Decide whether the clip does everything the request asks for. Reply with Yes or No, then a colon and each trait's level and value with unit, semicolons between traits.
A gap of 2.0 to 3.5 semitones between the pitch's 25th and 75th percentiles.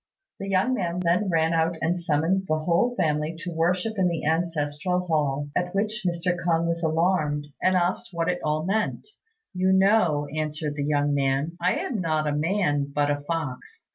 Yes: average, 3.2 semitones